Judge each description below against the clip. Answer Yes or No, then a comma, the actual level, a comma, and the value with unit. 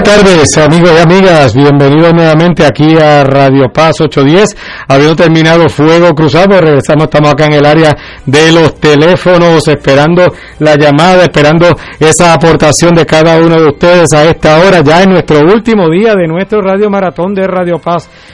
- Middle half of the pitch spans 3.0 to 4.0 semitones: No, narrow, 2.6 semitones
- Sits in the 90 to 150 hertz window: No, medium, 160 Hz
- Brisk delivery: No, average, 165 wpm